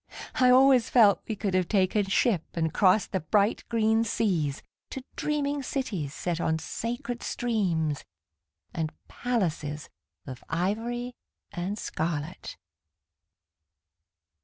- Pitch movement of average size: No, wide, 6.4 semitones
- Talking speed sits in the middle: No, slow, 110 wpm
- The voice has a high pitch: Yes, high, 200 Hz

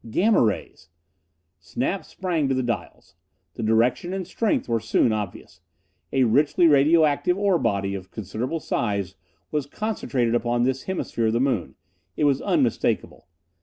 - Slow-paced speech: No, average, 150 wpm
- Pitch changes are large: Yes, wide, 6.1 semitones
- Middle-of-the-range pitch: No, low, 125 Hz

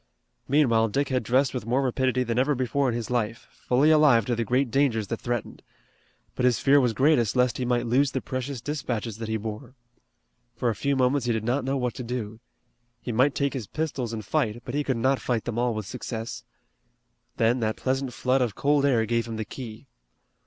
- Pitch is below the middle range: Yes, low, 125 Hz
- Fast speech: Yes, fast, 215 wpm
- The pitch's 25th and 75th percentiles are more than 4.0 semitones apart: No, average, 2.8 semitones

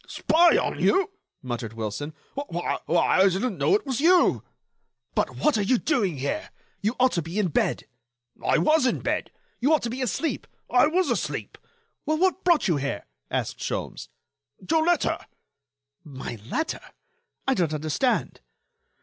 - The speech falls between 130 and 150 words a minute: No, average, 160 wpm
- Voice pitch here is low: No, high, 245 Hz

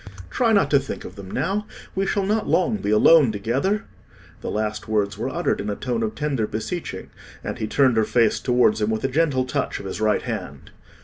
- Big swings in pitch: Yes, wide, 7.4 semitones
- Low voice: Yes, low, 125 Hz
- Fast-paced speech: Yes, fast, 220 wpm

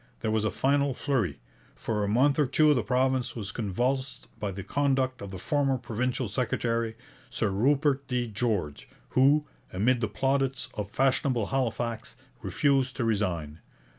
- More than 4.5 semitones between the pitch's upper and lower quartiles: No, average, 4.0 semitones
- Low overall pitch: Yes, low, 125 Hz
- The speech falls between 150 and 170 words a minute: Yes, average, 155 wpm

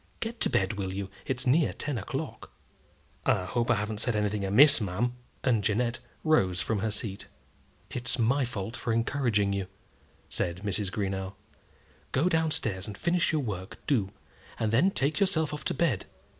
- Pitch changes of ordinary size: No, wide, 5.7 semitones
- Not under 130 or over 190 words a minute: Yes, average, 170 wpm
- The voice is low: Yes, low, 115 Hz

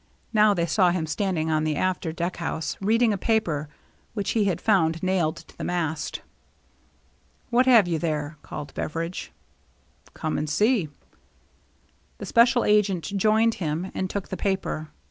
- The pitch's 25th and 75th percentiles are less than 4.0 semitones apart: No, average, 4.8 semitones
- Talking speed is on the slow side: No, average, 165 wpm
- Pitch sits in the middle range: Yes, medium, 180 Hz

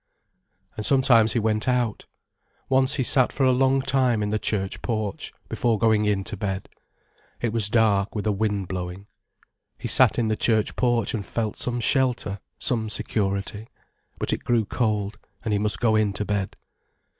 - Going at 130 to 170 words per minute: No, average, 180 wpm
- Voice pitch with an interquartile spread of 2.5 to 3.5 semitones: Yes, average, 2.8 semitones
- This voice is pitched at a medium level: No, low, 110 Hz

